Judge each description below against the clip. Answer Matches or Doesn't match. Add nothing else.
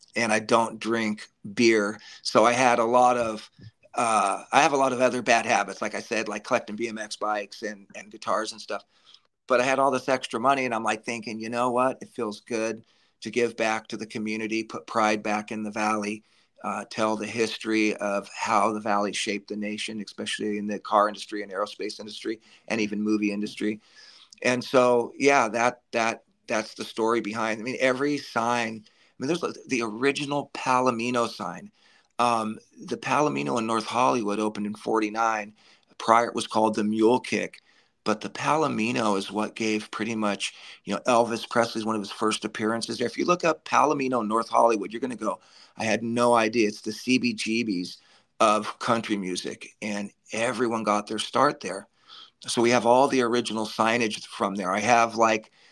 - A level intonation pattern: Matches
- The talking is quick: Doesn't match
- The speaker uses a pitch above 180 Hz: Doesn't match